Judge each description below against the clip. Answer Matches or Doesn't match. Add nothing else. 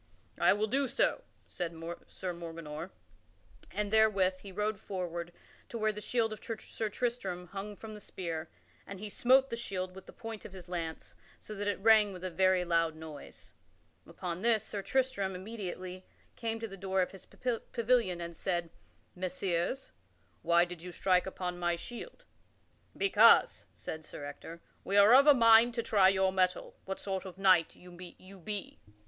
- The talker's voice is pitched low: Doesn't match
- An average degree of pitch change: Matches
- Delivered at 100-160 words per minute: Doesn't match